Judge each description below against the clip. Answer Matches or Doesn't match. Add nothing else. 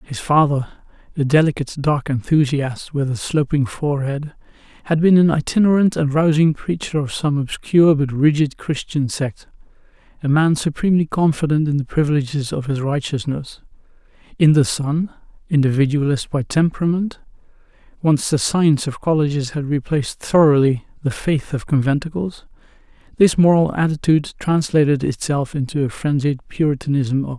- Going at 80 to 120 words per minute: Doesn't match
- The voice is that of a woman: Doesn't match